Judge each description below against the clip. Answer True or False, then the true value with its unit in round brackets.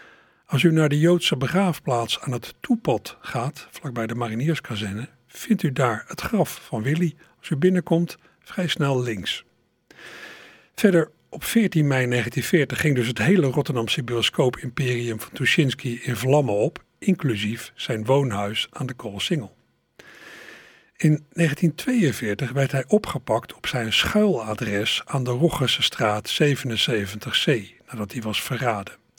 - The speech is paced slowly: True (130 wpm)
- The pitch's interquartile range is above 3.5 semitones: True (5.6 semitones)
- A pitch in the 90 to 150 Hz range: True (135 Hz)